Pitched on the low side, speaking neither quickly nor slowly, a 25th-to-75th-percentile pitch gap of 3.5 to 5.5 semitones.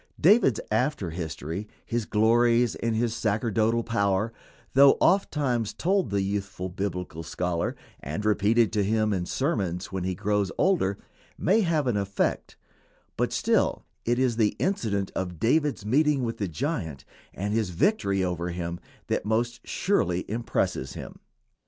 Yes: low, 105 Hz; average, 145 wpm; average, 4.4 semitones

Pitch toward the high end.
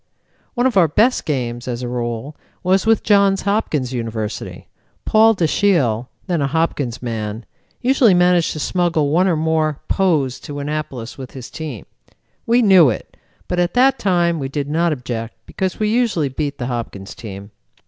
No: medium, 155 Hz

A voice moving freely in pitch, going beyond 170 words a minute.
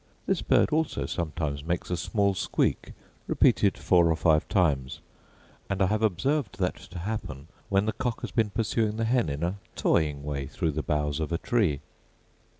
Yes: wide, 5.9 semitones; average, 180 wpm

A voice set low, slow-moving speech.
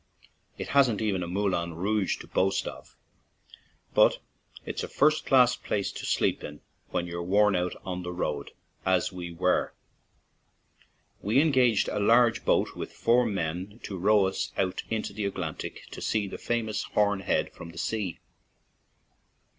No: low, 100 Hz; average, 160 wpm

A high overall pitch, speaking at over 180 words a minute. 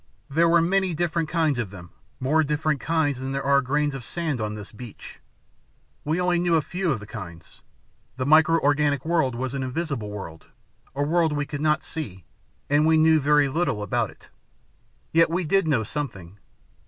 No: medium, 150 Hz; average, 190 wpm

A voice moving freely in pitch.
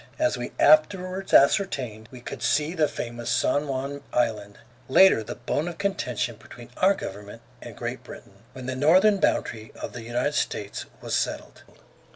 Yes: wide, 6.1 semitones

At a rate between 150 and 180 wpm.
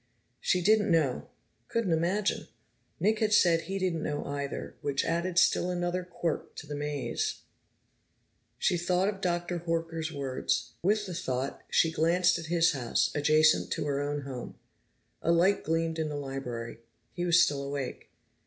Yes: average, 160 wpm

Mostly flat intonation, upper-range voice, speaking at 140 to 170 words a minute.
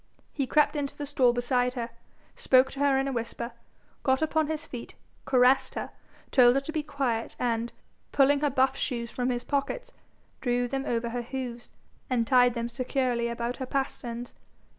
No: narrow, 2.3 semitones; very high, 255 Hz; average, 180 wpm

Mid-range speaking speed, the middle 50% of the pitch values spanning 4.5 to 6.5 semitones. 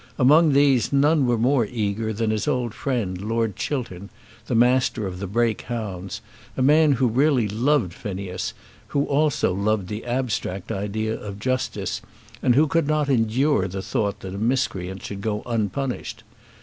Yes: average, 160 wpm; average, 4.8 semitones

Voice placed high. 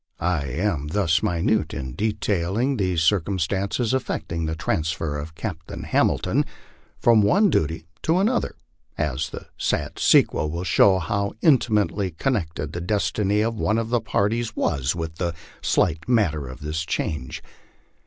No: very low, 90 Hz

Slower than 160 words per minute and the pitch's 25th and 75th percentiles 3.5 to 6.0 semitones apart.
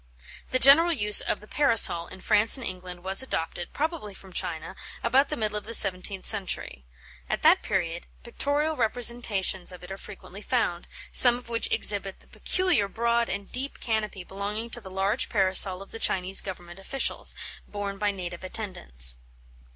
No: average, 170 wpm; average, 4.0 semitones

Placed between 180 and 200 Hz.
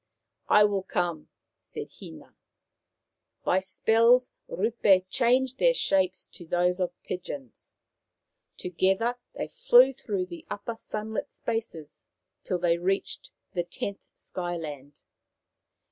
Yes: high, 190 Hz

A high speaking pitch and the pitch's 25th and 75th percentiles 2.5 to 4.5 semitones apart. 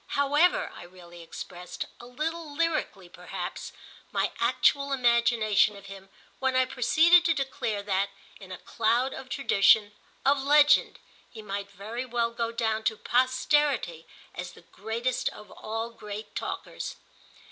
No: high, 235 Hz; average, 5.0 semitones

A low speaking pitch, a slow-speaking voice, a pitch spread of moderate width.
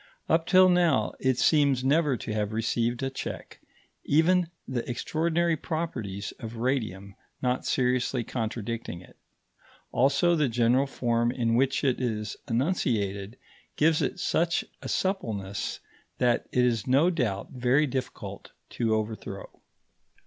Yes: low, 125 Hz; slow, 130 wpm; average, 4.8 semitones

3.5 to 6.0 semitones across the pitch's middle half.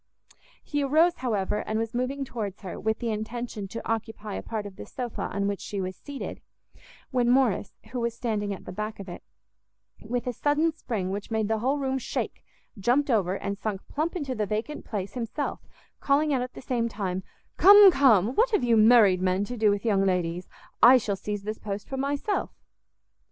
Yes: average, 4.4 semitones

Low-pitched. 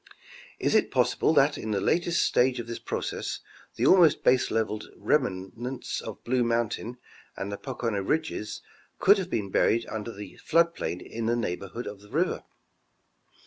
Yes: low, 115 Hz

